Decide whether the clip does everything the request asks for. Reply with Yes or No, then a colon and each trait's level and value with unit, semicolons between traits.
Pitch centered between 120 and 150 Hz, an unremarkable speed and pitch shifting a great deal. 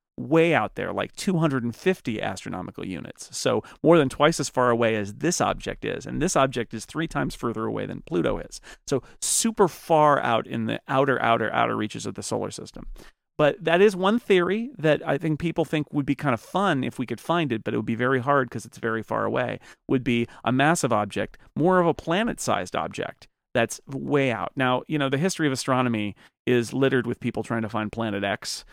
No: low, 135 Hz; fast, 215 wpm; wide, 5.8 semitones